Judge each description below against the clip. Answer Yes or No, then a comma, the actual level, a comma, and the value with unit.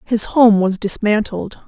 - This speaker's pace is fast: No, average, 145 wpm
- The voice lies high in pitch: Yes, high, 210 Hz